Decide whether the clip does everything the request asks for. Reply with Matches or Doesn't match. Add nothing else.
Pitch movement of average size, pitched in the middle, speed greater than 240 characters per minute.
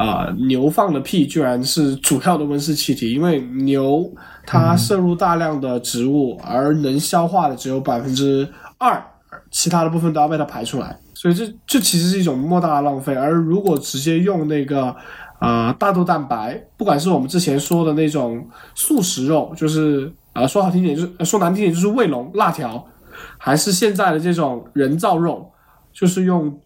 Matches